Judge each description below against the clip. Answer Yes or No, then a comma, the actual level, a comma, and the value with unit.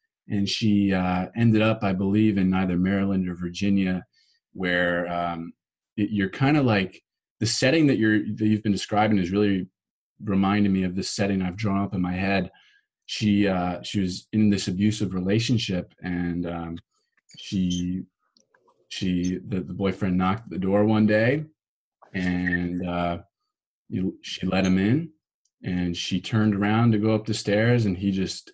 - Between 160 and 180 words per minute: Yes, average, 165 wpm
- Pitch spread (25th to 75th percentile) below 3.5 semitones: Yes, average, 2.8 semitones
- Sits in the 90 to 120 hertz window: Yes, low, 100 Hz